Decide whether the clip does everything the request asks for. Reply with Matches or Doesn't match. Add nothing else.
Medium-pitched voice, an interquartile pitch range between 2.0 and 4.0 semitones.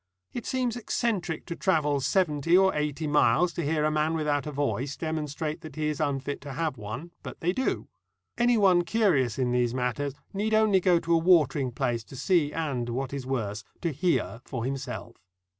Doesn't match